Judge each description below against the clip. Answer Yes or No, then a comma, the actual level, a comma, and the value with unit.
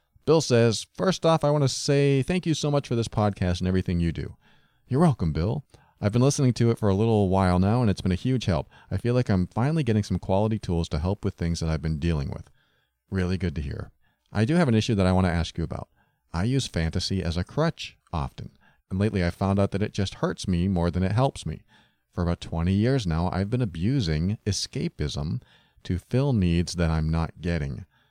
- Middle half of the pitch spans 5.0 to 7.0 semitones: Yes, wide, 5.6 semitones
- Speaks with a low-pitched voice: Yes, very low, 95 Hz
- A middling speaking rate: No, fast, 235 wpm